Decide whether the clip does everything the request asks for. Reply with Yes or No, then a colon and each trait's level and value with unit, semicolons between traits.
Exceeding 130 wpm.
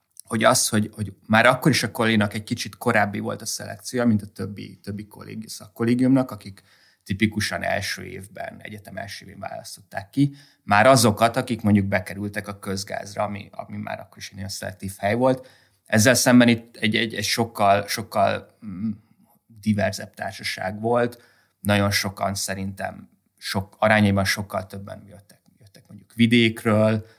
Yes: average, 150 wpm